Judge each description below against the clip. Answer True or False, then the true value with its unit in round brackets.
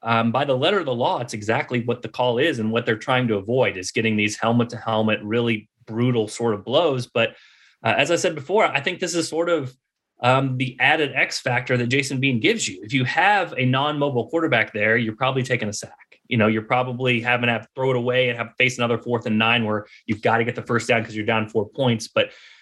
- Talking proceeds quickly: True (255 wpm)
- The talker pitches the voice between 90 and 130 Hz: True (120 Hz)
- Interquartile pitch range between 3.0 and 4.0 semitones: False (2.4 semitones)